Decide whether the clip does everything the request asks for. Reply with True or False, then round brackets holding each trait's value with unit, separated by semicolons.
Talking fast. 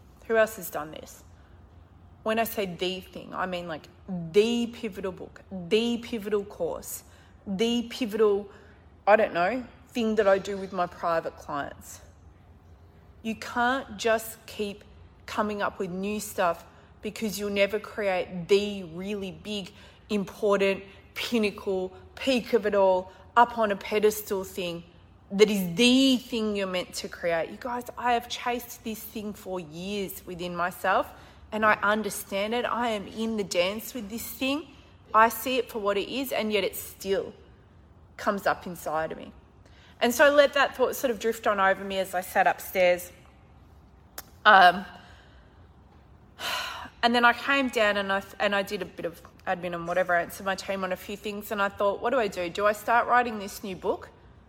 False (175 wpm)